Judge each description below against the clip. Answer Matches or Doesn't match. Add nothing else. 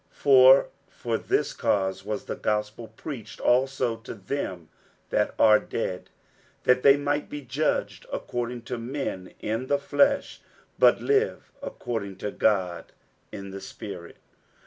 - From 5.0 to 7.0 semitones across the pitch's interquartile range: Matches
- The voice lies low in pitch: Matches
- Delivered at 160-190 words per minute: Doesn't match